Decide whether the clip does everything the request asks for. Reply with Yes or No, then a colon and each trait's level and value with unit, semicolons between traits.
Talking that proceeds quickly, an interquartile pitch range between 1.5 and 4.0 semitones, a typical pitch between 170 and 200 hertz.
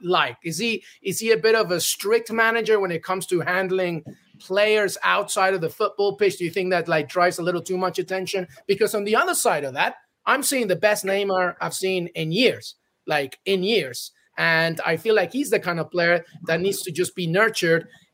Yes: fast, 220 wpm; average, 3.2 semitones; medium, 185 Hz